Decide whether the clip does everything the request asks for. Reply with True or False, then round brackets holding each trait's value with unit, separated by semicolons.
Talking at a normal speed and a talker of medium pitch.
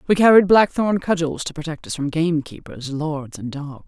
True (185 wpm; 160 Hz)